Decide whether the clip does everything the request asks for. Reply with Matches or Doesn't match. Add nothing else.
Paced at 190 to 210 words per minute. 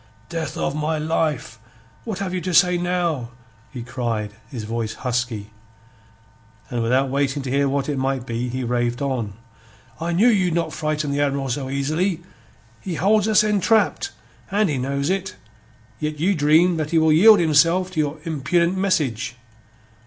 Doesn't match